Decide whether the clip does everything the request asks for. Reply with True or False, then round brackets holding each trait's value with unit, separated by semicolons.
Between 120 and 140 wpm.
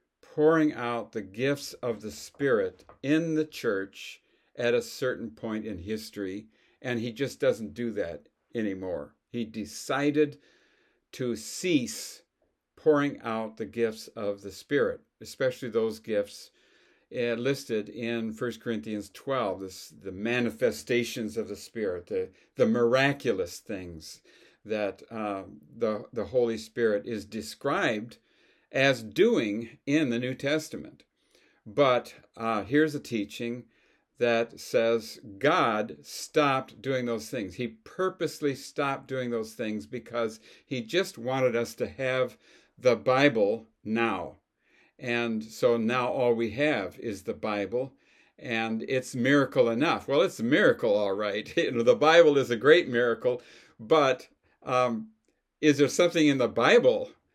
True (135 wpm)